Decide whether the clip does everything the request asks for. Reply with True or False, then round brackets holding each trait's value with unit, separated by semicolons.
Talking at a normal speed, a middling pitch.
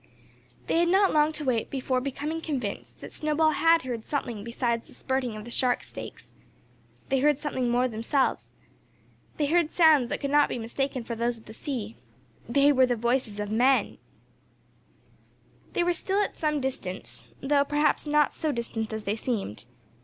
False (175 wpm; 265 Hz)